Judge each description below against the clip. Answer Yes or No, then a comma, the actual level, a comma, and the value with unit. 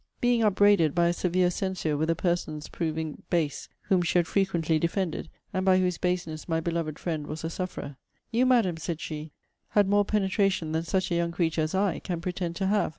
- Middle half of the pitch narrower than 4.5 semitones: Yes, average, 2.8 semitones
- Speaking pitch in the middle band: Yes, medium, 175 Hz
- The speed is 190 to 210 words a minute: Yes, fast, 205 wpm